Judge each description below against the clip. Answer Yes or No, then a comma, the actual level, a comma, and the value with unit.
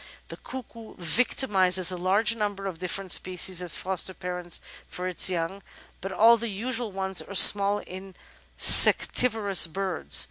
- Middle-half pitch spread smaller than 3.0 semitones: Yes, narrow, 2.5 semitones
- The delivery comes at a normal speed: Yes, average, 145 wpm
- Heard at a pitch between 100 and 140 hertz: No, high, 190 Hz